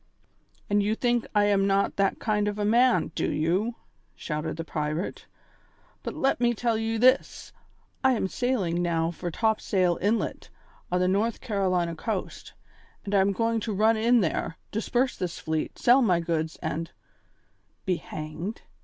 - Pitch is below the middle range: No, high, 200 Hz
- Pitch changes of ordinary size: Yes, average, 4.7 semitones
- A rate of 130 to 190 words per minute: Yes, average, 165 wpm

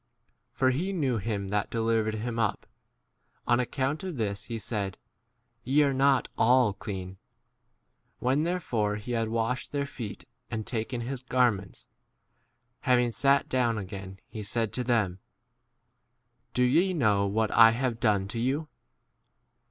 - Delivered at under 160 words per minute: Yes, average, 150 wpm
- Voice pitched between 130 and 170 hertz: No, low, 115 Hz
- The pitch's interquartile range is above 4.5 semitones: No, average, 3.6 semitones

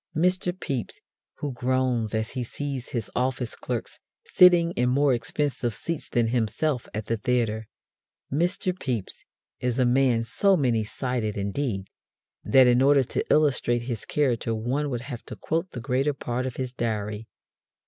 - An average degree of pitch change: Yes, average, 3.6 semitones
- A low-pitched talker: Yes, low, 125 Hz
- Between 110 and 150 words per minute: No, average, 160 wpm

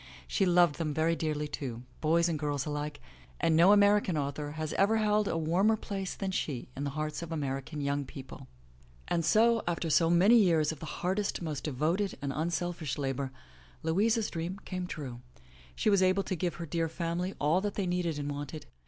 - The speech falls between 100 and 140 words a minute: No, average, 195 wpm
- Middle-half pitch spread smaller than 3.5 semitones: No, average, 4.0 semitones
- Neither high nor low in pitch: Yes, medium, 165 Hz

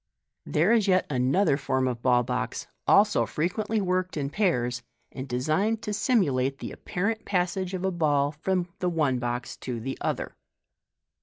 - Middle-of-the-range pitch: Yes, medium, 160 Hz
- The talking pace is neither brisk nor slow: Yes, average, 160 wpm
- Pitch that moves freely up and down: Yes, wide, 6.6 semitones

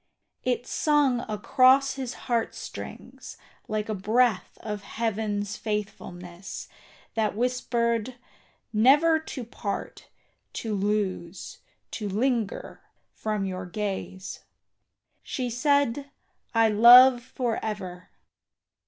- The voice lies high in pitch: Yes, high, 220 Hz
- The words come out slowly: Yes, slow, 95 wpm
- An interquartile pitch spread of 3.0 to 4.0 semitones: Yes, average, 3.5 semitones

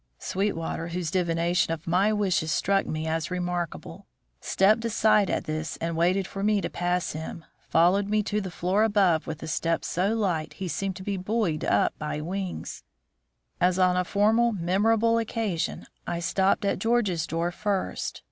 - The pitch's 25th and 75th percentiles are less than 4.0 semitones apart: Yes, average, 3.6 semitones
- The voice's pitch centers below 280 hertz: Yes, medium, 185 Hz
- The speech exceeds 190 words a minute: No, average, 170 wpm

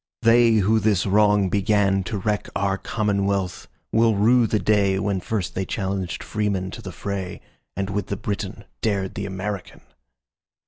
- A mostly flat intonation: Yes, narrow, 1.8 semitones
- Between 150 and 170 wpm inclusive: No, average, 140 wpm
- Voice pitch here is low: Yes, low, 100 Hz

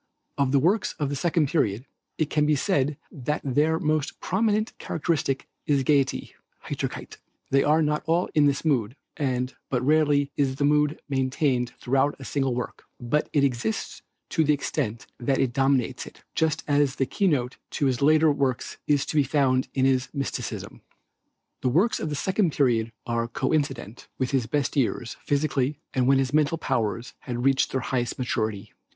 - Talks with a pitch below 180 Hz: Yes, medium, 140 Hz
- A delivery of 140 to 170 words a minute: No, average, 180 wpm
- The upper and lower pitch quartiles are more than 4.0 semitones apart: No, average, 2.8 semitones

